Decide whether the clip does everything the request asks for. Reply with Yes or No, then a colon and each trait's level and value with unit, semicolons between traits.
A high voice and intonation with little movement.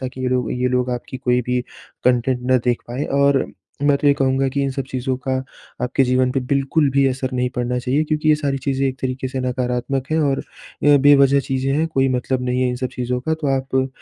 No: low, 130 Hz; narrow, 1.5 semitones